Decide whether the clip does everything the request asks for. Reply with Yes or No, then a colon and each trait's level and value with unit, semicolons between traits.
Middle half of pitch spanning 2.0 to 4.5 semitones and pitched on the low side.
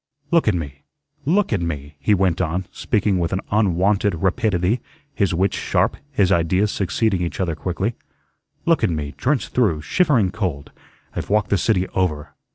Yes: average, 3.9 semitones; very low, 95 Hz